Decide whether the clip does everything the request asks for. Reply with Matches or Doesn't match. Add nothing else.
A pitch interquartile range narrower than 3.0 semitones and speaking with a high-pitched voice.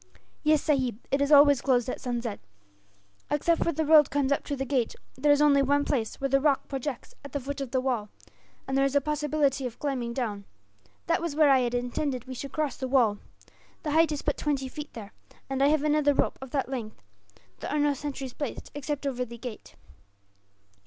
Matches